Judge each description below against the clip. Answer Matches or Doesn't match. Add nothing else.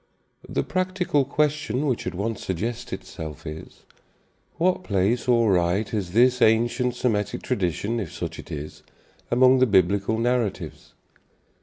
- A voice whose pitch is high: Doesn't match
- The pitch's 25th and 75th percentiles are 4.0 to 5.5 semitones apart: Matches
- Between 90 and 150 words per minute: Matches